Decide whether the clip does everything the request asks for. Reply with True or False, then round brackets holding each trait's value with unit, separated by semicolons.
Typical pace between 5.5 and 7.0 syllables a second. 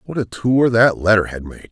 False (5.2 syllables/s)